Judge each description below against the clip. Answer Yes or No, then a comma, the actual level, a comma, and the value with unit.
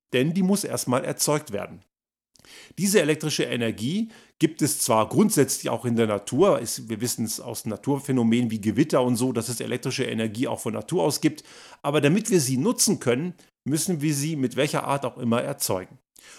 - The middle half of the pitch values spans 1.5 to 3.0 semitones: No, average, 4.9 semitones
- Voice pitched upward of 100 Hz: Yes, low, 135 Hz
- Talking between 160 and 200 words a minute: Yes, average, 185 wpm